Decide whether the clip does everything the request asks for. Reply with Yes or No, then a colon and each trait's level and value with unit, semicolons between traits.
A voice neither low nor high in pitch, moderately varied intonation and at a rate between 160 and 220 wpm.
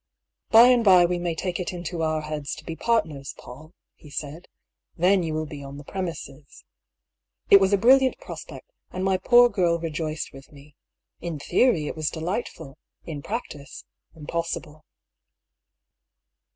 Yes: medium, 165 Hz; average, 3.9 semitones; average, 165 wpm